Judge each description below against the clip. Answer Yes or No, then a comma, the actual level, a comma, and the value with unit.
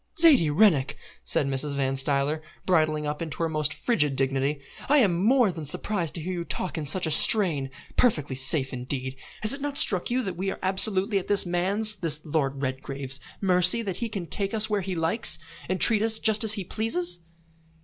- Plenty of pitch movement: Yes, wide, 6.1 semitones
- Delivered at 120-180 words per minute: No, average, 200 wpm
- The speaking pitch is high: No, medium, 175 Hz